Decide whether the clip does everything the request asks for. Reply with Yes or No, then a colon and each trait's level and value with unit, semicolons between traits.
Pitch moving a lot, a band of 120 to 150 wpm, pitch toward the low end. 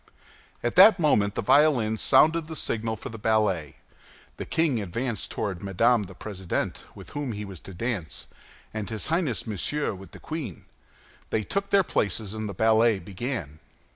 No: wide, 5.7 semitones; average, 170 wpm; low, 110 Hz